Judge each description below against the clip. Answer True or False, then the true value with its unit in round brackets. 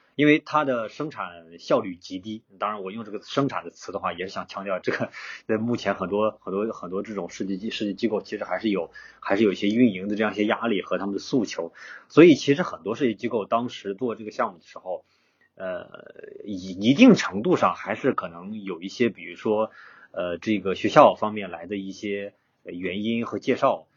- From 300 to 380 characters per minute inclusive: True (315 characters per minute)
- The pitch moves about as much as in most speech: True (3.4 semitones)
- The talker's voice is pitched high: False (110 Hz)